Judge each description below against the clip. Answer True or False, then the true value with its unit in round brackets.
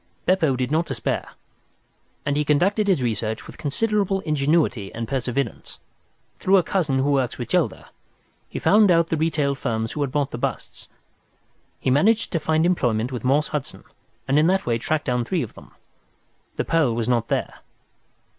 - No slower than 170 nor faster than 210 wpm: True (175 wpm)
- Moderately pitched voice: True (145 Hz)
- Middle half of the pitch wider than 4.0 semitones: True (5.1 semitones)